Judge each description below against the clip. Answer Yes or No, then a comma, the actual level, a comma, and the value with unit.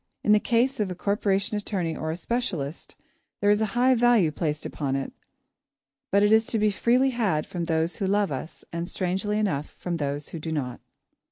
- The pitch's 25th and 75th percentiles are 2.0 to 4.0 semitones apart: No, average, 5.0 semitones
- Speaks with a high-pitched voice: Yes, high, 195 Hz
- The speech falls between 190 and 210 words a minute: Yes, average, 200 wpm